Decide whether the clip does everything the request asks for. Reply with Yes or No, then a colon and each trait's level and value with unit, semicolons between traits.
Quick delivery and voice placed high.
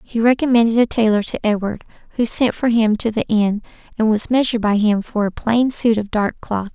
Yes: fast, 220 wpm; high, 220 Hz